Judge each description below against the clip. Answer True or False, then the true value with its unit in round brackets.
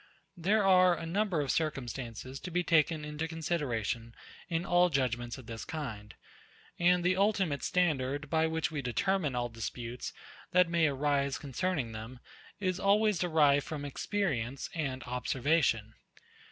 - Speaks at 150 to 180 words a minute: False (140 wpm)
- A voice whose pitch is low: False (150 Hz)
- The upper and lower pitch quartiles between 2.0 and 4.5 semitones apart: False (5.6 semitones)